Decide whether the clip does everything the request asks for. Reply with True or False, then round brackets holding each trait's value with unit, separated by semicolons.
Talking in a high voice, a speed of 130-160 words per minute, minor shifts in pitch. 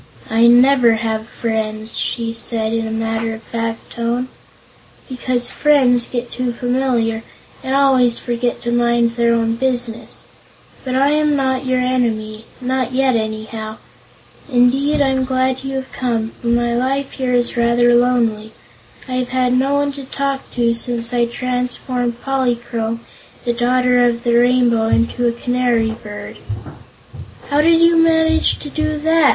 True (245 Hz; 150 wpm; 2.0 semitones)